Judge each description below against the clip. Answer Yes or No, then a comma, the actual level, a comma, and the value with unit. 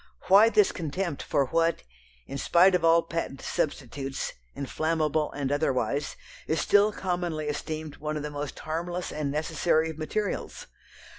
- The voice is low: No, medium, 155 Hz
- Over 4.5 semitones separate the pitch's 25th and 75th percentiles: No, average, 2.9 semitones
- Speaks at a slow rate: No, average, 145 wpm